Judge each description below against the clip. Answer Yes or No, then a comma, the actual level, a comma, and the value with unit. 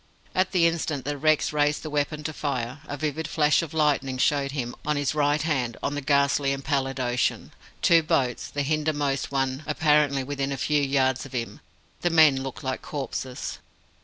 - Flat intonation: Yes, narrow, 2.2 semitones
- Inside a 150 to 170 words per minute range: No, average, 190 wpm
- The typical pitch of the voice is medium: Yes, medium, 145 Hz